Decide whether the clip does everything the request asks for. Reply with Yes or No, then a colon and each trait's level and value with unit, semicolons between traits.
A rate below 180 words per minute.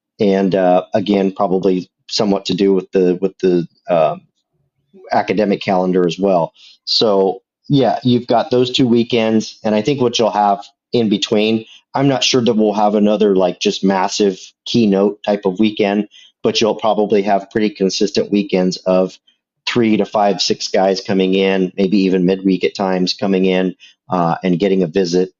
Yes: average, 170 wpm